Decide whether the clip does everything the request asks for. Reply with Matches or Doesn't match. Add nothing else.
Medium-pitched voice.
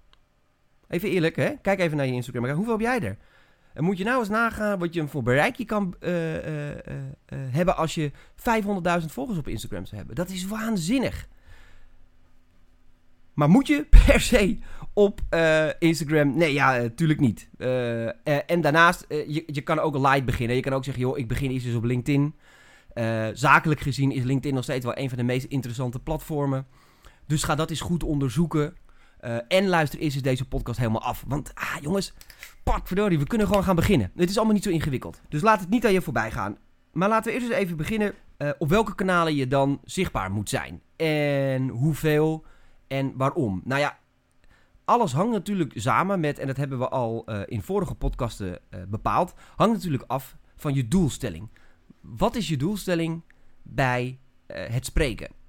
Matches